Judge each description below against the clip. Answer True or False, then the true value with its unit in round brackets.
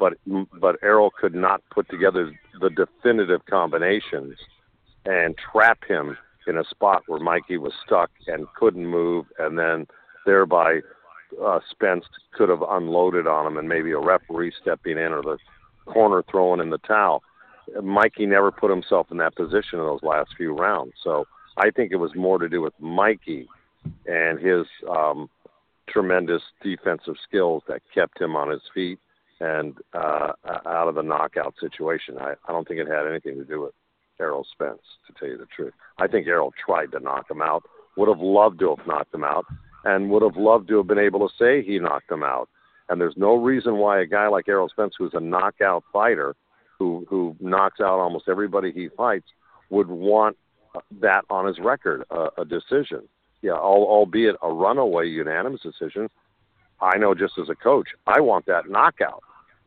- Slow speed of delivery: False (180 wpm)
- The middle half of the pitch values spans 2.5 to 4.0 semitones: True (3.5 semitones)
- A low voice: True (95 Hz)